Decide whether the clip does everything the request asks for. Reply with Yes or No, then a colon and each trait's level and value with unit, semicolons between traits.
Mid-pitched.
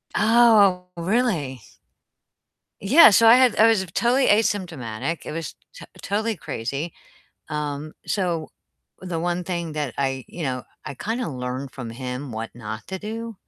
Yes: medium, 170 Hz